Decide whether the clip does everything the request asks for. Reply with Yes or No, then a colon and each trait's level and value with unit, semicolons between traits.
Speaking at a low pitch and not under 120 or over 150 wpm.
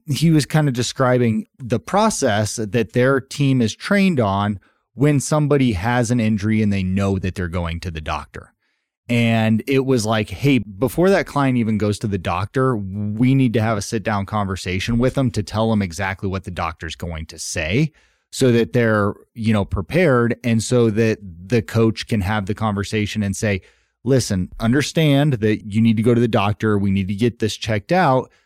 No: low, 110 Hz; average, 200 wpm